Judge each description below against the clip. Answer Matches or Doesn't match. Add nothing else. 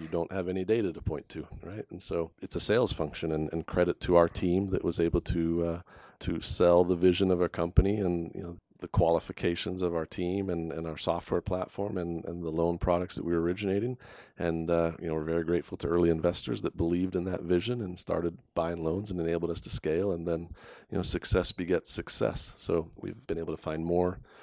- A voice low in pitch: Matches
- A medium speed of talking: Doesn't match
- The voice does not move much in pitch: Matches